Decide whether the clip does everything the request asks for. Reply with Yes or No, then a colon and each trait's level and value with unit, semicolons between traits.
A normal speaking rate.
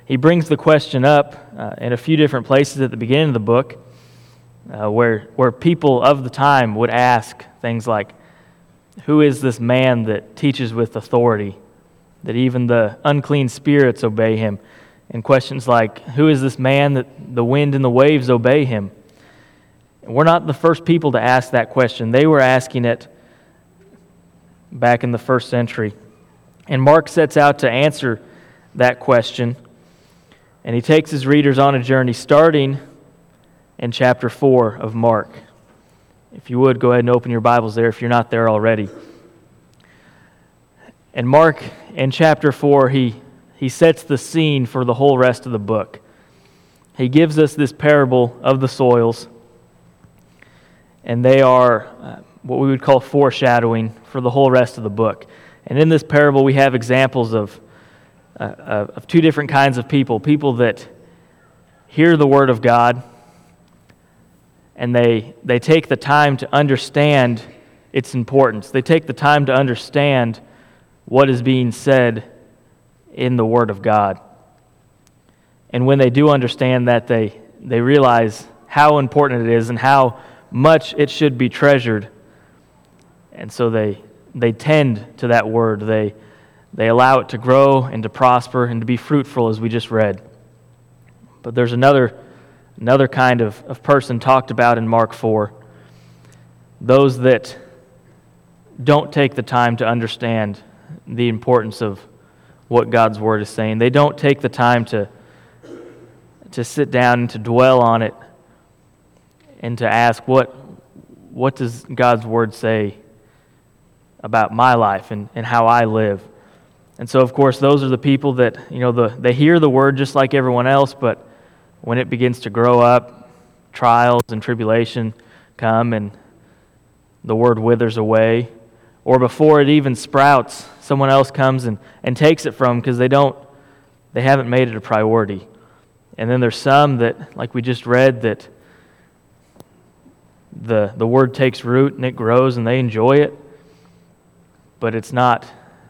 Yes: average, 160 wpm